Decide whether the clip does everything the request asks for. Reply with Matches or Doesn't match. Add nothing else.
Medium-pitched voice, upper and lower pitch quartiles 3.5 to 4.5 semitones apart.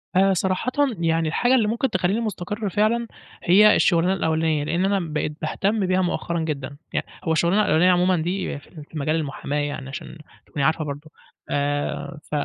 Matches